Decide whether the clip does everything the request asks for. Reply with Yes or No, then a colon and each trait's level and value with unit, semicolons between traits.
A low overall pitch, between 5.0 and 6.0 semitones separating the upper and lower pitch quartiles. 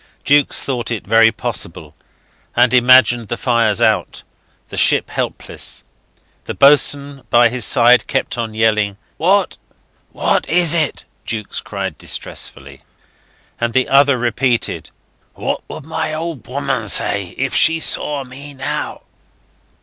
No: low, 125 Hz; average, 3.7 semitones